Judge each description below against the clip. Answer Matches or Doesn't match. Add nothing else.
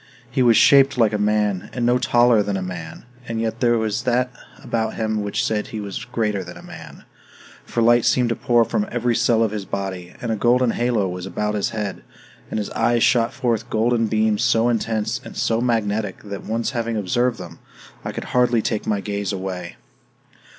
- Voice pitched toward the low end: Matches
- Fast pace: Matches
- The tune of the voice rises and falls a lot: Doesn't match